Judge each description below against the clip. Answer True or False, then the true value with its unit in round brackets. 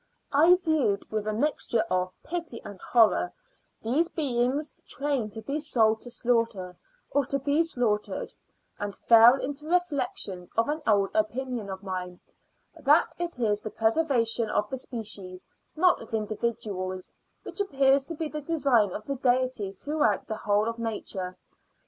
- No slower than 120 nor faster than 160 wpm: True (150 wpm)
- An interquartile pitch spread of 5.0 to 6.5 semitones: True (5.4 semitones)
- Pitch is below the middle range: False (235 Hz)